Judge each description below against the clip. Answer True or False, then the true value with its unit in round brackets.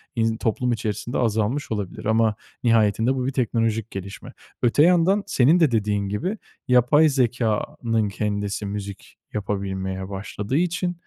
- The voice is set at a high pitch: False (115 Hz)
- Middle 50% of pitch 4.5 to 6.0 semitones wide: False (3.8 semitones)